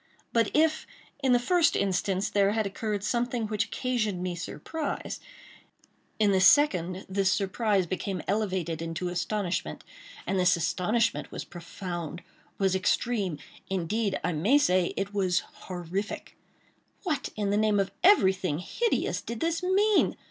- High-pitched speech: Yes, high, 200 Hz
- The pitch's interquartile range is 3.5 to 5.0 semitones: Yes, average, 4.1 semitones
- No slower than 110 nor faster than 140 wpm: Yes, slow, 135 wpm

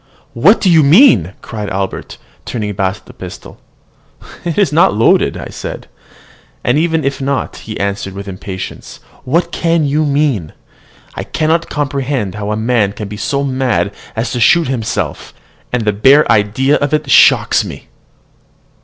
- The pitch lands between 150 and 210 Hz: No, low, 130 Hz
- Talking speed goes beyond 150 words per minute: Yes, average, 160 wpm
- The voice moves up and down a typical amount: No, wide, 6.3 semitones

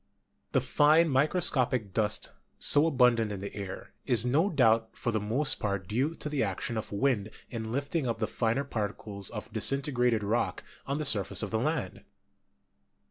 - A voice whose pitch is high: No, low, 120 Hz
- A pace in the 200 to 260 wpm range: No, average, 175 wpm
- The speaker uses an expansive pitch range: No, average, 4.7 semitones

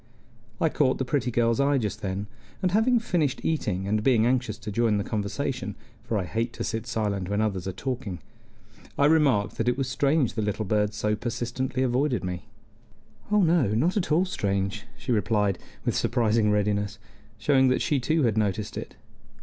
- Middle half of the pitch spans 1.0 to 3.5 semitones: No, average, 4.5 semitones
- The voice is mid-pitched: No, low, 115 Hz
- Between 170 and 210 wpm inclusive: Yes, average, 185 wpm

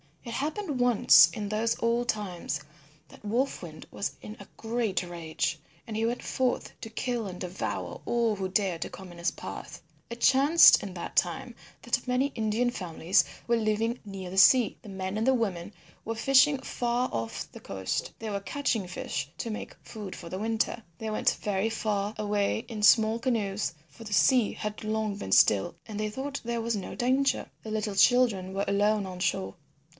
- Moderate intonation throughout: Yes, average, 3.5 semitones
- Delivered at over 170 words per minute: Yes, average, 190 wpm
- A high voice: Yes, high, 215 Hz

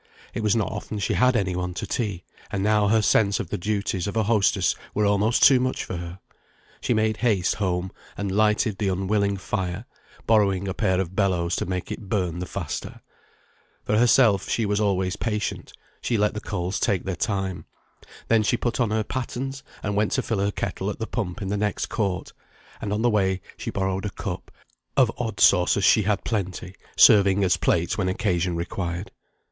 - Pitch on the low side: Yes, low, 100 Hz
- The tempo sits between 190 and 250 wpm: Yes, average, 200 wpm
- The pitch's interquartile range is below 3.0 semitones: Yes, narrow, 2.6 semitones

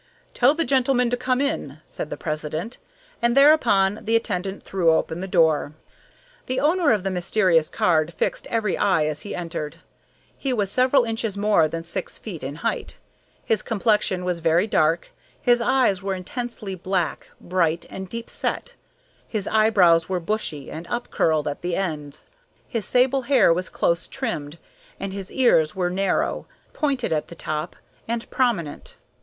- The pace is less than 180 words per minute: Yes, average, 165 wpm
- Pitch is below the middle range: No, high, 195 Hz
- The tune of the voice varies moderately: No, wide, 6.0 semitones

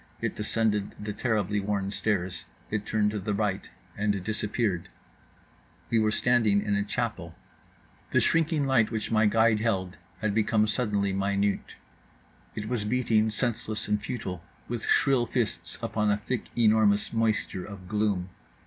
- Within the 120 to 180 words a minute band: Yes, average, 150 wpm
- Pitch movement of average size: No, narrow, 1.8 semitones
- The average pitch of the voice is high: No, low, 105 Hz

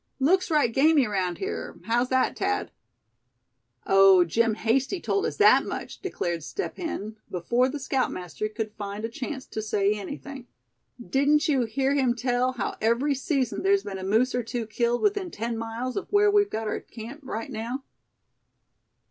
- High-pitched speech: Yes, high, 245 Hz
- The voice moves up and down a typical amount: Yes, average, 4.4 semitones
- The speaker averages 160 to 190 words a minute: Yes, average, 170 wpm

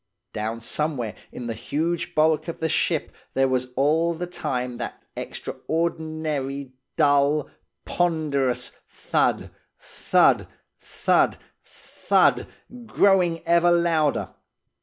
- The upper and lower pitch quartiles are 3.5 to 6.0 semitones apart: Yes, average, 3.9 semitones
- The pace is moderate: No, slow, 100 wpm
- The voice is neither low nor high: Yes, medium, 155 Hz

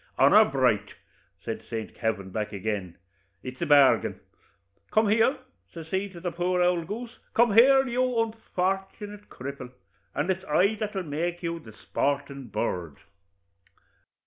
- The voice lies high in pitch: No, medium, 175 Hz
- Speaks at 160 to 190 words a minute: No, average, 145 wpm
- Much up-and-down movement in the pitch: Yes, wide, 8.1 semitones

